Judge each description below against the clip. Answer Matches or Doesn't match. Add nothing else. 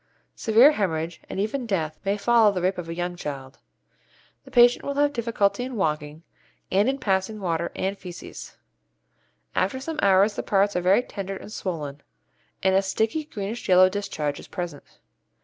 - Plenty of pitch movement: Doesn't match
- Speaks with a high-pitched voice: Matches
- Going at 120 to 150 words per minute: Doesn't match